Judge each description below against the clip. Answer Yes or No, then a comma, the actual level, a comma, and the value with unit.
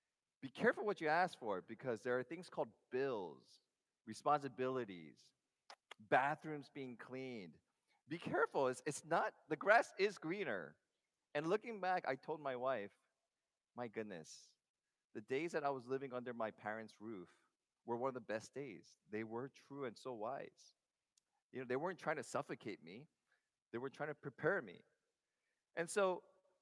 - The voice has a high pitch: No, medium, 140 Hz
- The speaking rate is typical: Yes, average, 160 wpm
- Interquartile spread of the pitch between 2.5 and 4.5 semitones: No, wide, 5.6 semitones